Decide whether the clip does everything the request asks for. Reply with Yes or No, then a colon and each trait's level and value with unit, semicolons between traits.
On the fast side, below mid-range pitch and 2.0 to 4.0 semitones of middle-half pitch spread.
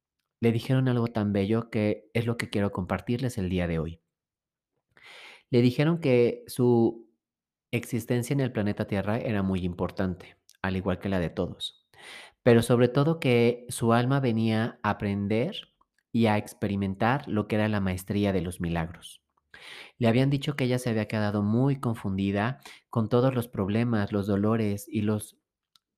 No: average, 165 wpm; low, 110 Hz; average, 3.3 semitones